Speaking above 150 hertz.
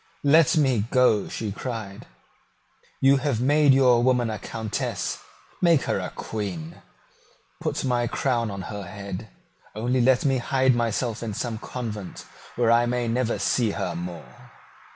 No: low, 120 Hz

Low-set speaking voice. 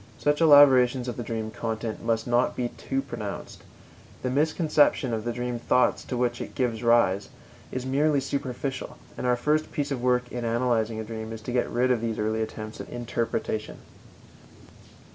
Yes: low, 120 Hz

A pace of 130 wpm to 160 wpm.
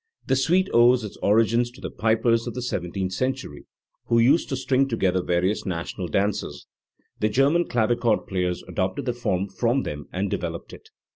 No: average, 170 wpm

